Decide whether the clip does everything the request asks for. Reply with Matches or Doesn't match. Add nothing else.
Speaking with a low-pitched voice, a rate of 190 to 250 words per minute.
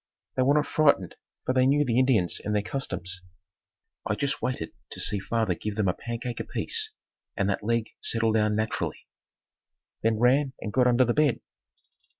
Doesn't match